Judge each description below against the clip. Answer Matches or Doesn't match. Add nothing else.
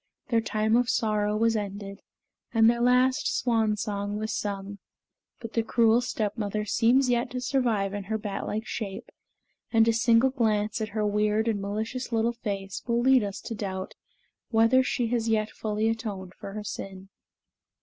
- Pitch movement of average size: Doesn't match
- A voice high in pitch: Matches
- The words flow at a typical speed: Matches